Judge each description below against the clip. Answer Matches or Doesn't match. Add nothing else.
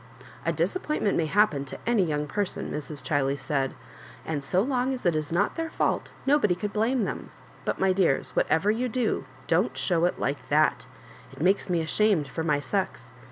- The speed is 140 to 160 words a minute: Doesn't match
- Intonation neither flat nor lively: Doesn't match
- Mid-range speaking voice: Matches